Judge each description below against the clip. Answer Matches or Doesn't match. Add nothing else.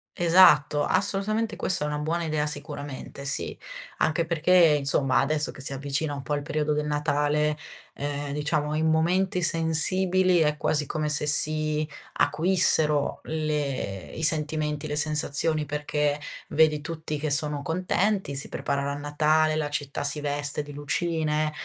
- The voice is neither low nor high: Matches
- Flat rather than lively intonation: Matches